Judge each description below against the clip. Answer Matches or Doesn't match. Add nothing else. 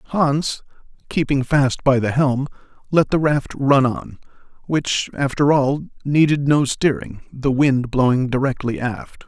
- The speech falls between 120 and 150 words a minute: Matches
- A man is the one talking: Matches